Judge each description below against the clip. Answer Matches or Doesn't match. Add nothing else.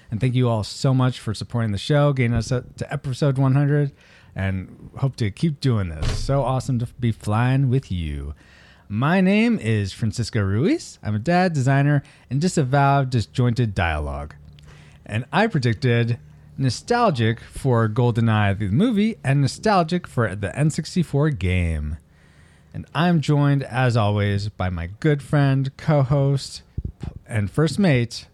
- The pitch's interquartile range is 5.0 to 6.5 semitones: Matches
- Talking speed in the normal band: Matches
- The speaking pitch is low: Matches